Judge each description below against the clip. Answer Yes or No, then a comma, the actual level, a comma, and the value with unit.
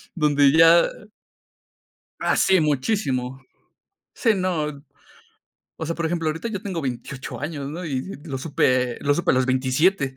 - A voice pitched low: No, medium, 150 Hz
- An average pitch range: Yes, average, 4.2 semitones